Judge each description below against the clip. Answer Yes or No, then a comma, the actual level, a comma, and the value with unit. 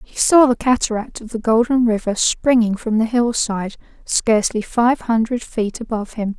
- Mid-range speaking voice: No, high, 230 Hz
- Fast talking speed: No, average, 170 wpm